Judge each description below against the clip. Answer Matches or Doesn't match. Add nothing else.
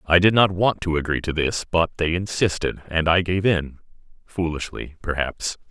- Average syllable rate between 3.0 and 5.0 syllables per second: Matches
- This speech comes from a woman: Doesn't match